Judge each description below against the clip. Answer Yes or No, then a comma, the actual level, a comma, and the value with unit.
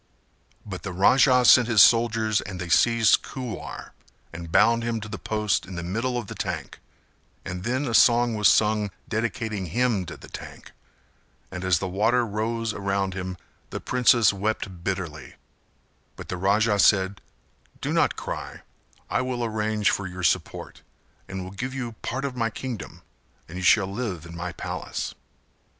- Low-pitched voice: Yes, low, 105 Hz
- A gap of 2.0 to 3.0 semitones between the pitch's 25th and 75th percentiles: No, average, 3.8 semitones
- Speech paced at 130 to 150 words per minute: No, average, 165 wpm